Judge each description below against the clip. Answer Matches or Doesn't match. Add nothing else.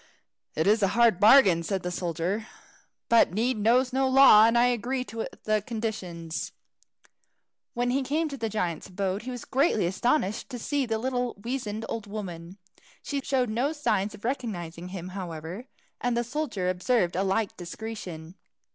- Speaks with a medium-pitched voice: Doesn't match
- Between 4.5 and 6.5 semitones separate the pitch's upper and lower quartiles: Matches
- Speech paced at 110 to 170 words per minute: Matches